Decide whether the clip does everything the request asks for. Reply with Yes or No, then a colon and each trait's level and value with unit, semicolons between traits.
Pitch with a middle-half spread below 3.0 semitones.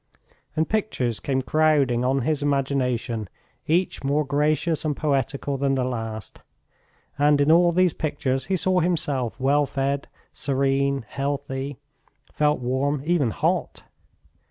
Yes: narrow, 2.4 semitones